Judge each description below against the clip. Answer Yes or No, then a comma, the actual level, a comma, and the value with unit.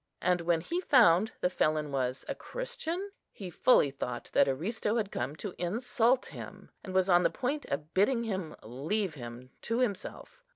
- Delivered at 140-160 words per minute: No, average, 175 wpm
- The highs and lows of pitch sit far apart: Yes, wide, 7.5 semitones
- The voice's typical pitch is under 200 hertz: Yes, medium, 185 Hz